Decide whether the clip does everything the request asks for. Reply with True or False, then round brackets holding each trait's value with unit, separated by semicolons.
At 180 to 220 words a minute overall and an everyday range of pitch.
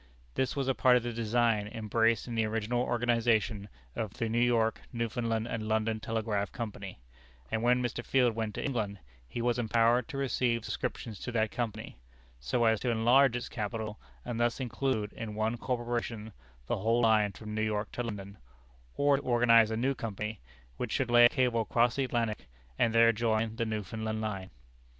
False (185 wpm; 1.8 semitones)